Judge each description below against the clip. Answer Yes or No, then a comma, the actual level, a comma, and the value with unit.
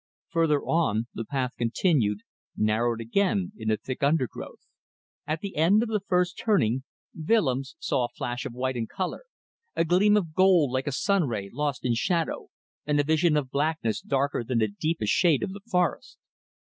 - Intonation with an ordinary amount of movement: No, wide, 6.5 semitones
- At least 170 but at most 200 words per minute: Yes, average, 180 wpm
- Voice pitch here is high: No, medium, 145 Hz